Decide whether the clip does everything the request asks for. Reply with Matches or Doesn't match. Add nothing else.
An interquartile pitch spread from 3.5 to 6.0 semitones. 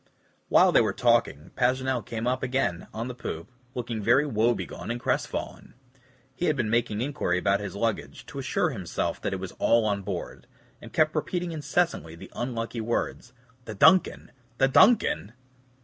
Matches